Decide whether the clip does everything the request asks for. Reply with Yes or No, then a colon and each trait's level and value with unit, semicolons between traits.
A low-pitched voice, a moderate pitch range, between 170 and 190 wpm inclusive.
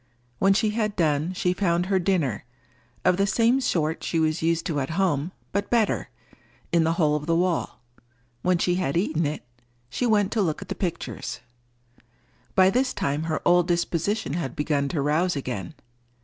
No: medium, 170 Hz; average, 4.3 semitones; average, 175 wpm